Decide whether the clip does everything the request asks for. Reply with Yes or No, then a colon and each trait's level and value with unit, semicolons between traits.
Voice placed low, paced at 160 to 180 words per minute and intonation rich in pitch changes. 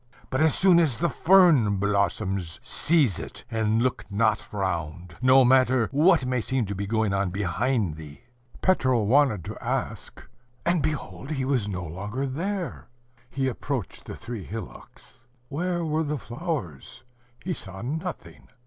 No: low, 125 Hz; average, 150 wpm; wide, 6.8 semitones